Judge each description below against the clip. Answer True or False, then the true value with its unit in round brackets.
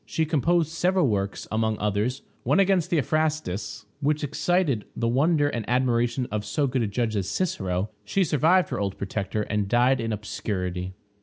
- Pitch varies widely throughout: True (6.9 semitones)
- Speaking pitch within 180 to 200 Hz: False (120 Hz)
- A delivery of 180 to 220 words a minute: False (165 wpm)